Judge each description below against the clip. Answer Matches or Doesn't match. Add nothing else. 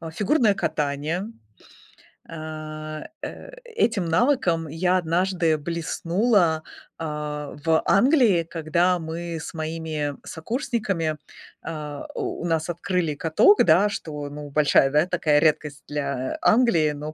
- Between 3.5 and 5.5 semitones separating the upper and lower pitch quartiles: Doesn't match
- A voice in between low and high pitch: Matches